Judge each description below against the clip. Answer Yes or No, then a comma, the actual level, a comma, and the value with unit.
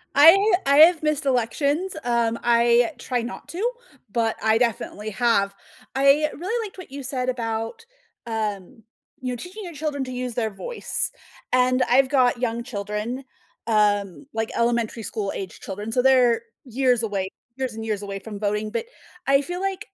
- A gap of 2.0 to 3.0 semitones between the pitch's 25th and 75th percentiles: No, average, 4.0 semitones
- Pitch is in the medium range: No, high, 245 Hz